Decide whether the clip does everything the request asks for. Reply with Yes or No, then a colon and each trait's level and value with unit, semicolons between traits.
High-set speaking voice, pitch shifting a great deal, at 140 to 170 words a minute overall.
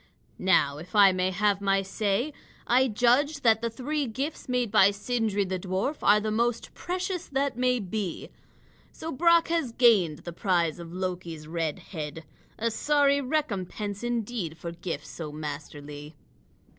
Yes: high, 205 Hz; wide, 6.1 semitones; average, 155 wpm